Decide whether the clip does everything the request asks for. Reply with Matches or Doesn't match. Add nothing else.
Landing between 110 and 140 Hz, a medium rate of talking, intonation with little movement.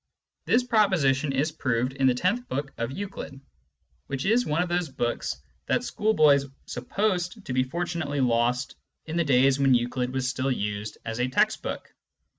Doesn't match